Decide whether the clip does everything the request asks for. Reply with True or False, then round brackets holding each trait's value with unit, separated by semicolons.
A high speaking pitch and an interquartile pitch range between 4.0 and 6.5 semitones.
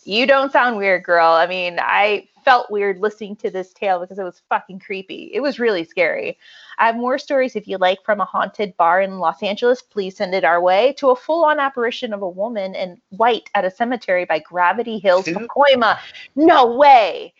True (210 Hz; 5.6 semitones)